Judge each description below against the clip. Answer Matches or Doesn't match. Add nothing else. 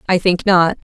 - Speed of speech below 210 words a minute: Matches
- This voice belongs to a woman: Matches